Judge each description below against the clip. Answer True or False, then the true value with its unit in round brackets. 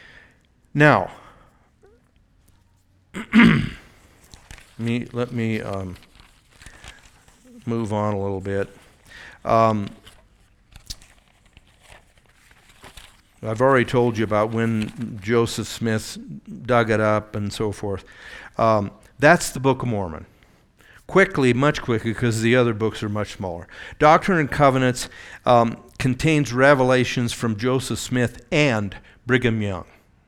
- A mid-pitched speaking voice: False (115 Hz)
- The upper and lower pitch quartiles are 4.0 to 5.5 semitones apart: False (3.6 semitones)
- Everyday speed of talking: False (105 wpm)